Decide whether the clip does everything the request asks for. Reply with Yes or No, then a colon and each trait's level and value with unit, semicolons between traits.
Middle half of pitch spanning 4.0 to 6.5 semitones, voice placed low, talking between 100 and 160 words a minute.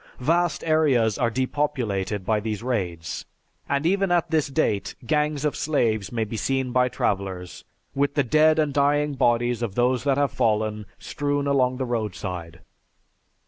Yes: average, 5.0 semitones; low, 125 Hz; average, 155 wpm